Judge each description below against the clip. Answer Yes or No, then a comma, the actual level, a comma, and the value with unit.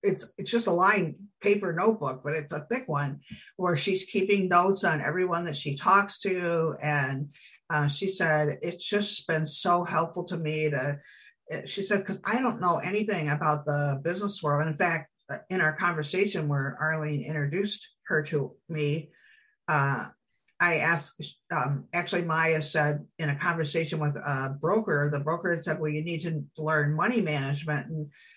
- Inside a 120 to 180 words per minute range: Yes, average, 175 wpm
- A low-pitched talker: No, medium, 165 Hz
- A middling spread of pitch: Yes, average, 4.0 semitones